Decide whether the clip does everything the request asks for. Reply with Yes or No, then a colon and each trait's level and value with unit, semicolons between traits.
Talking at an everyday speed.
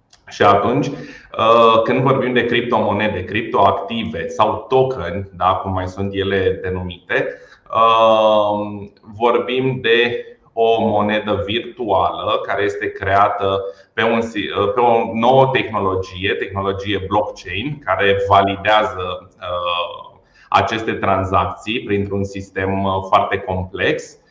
No: slow, 95 wpm